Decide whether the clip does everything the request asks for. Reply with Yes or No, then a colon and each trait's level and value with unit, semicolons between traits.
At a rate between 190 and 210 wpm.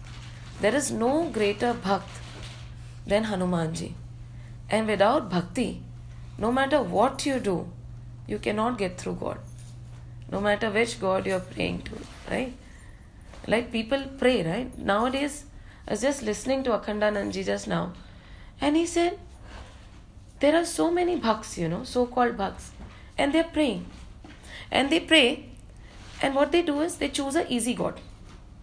No: average, 155 wpm